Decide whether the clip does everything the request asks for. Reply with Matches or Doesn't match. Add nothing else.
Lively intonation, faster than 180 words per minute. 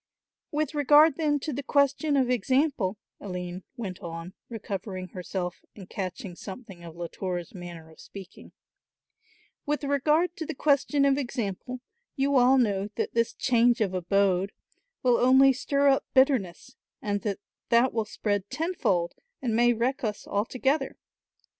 Doesn't match